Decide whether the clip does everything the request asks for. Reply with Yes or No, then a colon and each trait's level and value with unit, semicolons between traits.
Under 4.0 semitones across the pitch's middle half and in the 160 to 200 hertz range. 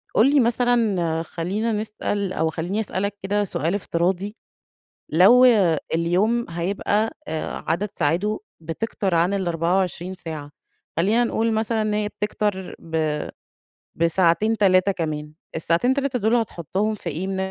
No: average, 4.3 semitones; high, 190 Hz